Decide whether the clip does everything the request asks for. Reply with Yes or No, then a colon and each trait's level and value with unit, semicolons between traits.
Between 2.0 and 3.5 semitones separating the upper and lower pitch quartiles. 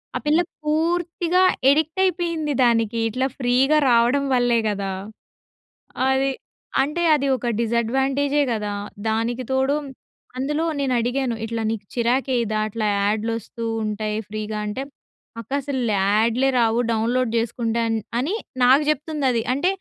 No: average, 3.9 semitones